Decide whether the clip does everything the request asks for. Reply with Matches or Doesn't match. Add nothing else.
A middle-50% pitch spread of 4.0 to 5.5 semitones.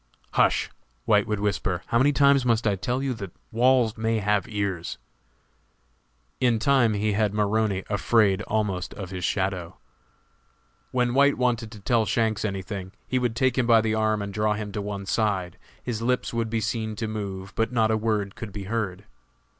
Doesn't match